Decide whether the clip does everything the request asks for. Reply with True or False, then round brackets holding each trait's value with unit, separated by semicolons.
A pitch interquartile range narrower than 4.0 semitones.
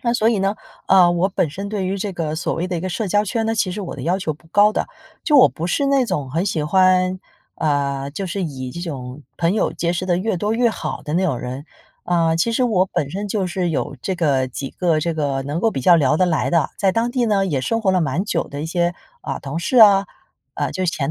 False (4.5 semitones)